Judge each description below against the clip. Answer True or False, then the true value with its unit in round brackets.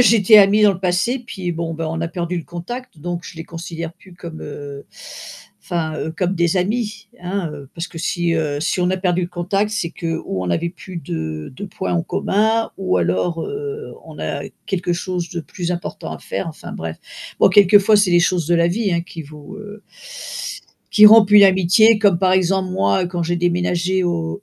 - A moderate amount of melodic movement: True (3.0 semitones)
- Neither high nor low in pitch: True (175 Hz)